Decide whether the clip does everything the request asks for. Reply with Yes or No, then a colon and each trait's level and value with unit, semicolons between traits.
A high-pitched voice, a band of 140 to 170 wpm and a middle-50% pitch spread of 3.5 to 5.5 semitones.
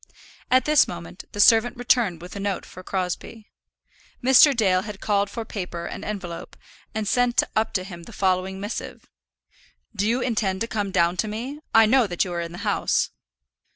No: high, 205 Hz; average, 190 wpm; average, 3.8 semitones